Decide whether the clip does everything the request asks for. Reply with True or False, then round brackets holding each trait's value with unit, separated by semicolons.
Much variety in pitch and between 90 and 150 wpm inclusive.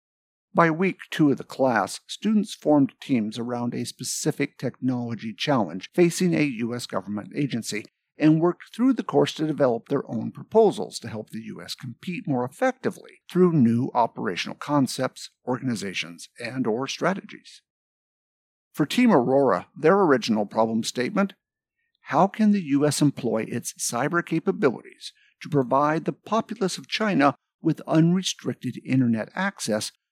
True (7.7 semitones; 135 wpm)